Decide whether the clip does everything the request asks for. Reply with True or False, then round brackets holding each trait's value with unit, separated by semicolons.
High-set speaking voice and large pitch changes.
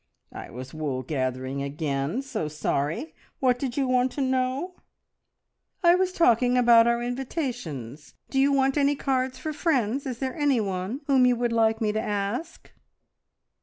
True (245 Hz; 6.8 semitones)